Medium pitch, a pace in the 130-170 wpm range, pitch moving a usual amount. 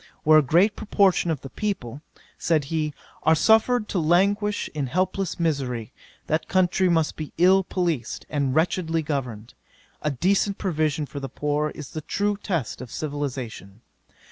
Yes: medium, 155 Hz; average, 155 wpm; average, 4.8 semitones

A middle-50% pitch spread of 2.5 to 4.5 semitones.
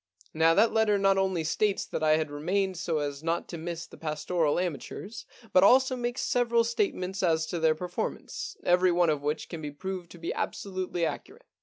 Yes: average, 3.7 semitones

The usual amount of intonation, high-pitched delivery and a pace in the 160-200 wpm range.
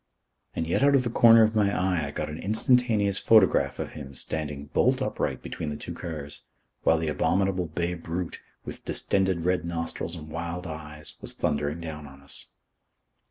No: average, 4.1 semitones; very low, 85 Hz; average, 180 wpm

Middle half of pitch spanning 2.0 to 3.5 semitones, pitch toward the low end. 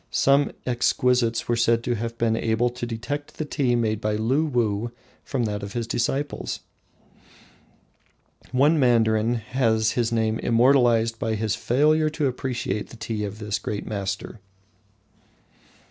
Yes: narrow, 2.4 semitones; low, 115 Hz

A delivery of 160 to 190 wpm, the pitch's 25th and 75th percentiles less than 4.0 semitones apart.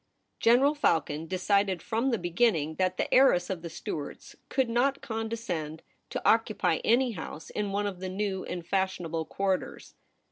No: average, 165 wpm; average, 4.9 semitones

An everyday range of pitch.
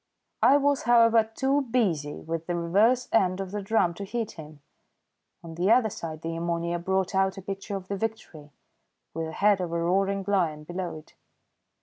Yes: average, 4.6 semitones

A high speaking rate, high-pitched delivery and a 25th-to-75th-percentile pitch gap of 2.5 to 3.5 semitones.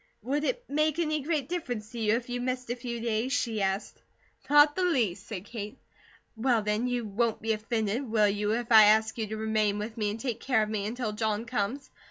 Yes: fast, 225 wpm; high, 230 Hz; average, 3.1 semitones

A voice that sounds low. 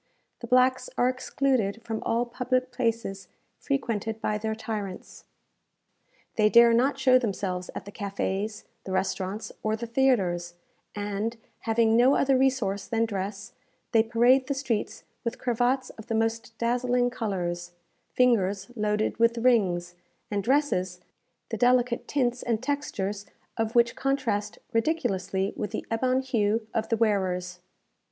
No: high, 225 Hz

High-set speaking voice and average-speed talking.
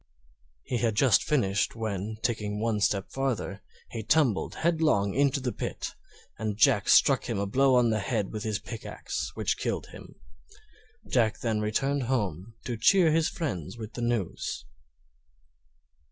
No: low, 115 Hz; average, 155 wpm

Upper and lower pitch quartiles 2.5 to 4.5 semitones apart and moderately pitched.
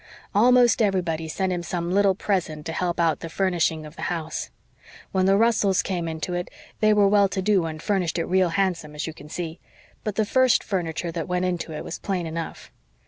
Yes: average, 3.2 semitones; medium, 180 Hz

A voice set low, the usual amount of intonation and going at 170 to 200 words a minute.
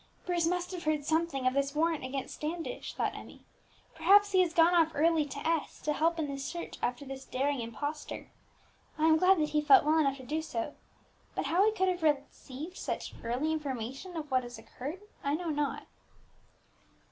No: very high, 305 Hz; average, 3.5 semitones; average, 195 wpm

